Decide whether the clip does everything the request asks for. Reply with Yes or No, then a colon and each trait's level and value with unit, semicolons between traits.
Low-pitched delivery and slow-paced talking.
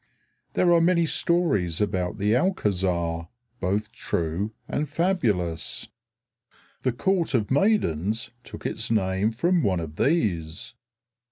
Yes: low, 105 Hz; slow, 115 wpm